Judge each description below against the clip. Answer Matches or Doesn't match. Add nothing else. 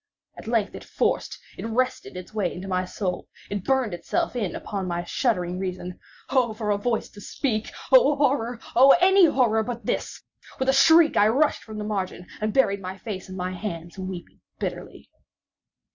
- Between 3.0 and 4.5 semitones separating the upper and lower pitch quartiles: Doesn't match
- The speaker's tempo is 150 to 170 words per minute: Matches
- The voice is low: Doesn't match